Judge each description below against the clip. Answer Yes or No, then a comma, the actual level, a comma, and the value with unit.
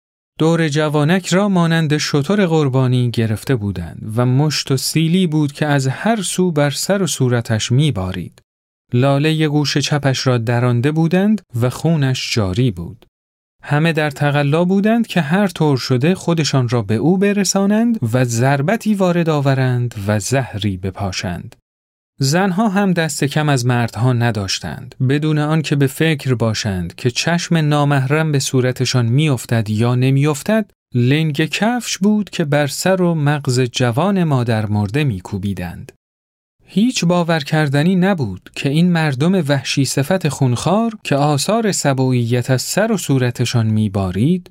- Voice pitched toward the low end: No, medium, 145 Hz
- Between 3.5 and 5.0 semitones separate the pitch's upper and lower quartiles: No, wide, 5.4 semitones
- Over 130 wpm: Yes, average, 140 wpm